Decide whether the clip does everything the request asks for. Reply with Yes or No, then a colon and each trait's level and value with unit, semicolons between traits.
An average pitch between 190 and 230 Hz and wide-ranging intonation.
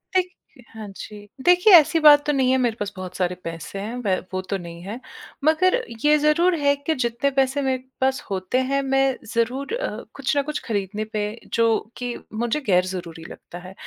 No: very high, 250 Hz; wide, 6.3 semitones